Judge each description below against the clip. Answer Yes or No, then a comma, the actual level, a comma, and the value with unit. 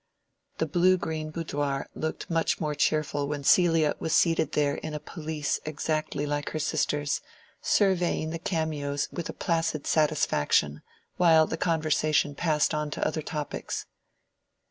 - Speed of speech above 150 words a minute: No, average, 145 wpm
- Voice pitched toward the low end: No, medium, 155 Hz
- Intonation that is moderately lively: No, narrow, 1.8 semitones